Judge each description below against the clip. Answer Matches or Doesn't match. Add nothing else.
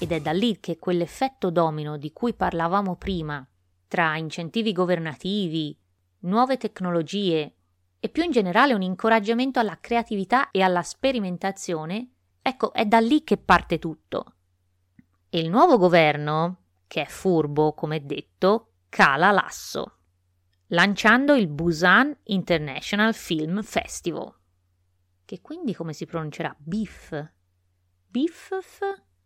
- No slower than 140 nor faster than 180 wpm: Doesn't match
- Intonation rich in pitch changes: Matches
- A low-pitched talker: Doesn't match